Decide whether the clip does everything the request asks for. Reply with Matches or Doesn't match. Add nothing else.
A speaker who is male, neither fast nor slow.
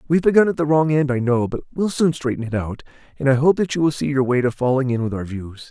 Doesn't match